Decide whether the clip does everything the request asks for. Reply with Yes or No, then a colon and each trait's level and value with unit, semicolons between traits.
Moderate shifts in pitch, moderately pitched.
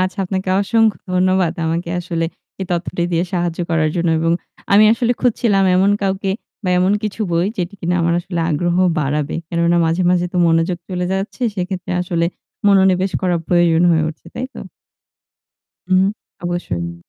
No: narrow, 2.2 semitones; medium, 180 Hz